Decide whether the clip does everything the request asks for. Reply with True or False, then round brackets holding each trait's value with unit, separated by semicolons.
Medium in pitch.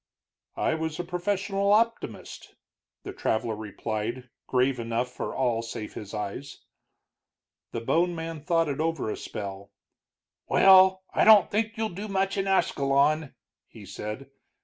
True (155 Hz)